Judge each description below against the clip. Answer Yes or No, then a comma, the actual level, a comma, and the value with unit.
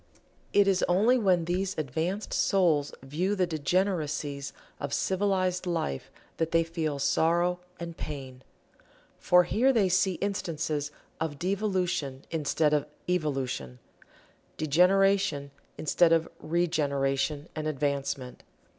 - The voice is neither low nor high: Yes, medium, 165 Hz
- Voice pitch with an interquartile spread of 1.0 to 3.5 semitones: No, average, 4.3 semitones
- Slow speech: Yes, slow, 110 wpm